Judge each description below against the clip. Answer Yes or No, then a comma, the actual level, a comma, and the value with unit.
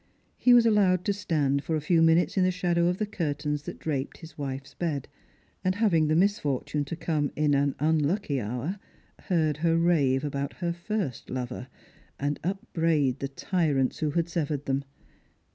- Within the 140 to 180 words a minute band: Yes, average, 175 wpm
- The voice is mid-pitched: Yes, medium, 155 Hz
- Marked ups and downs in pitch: No, average, 3.8 semitones